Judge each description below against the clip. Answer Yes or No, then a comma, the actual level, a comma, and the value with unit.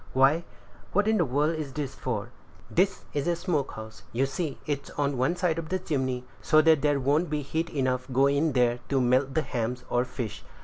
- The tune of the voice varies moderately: Yes, average, 3.8 semitones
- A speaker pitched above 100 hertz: Yes, medium, 140 Hz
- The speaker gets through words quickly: Yes, fast, 215 wpm